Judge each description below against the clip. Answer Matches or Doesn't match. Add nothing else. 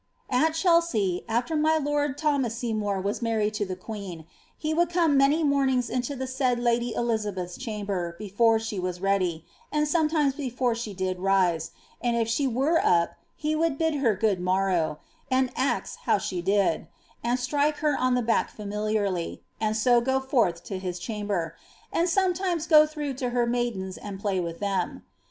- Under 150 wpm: Doesn't match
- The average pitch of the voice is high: Matches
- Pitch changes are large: Matches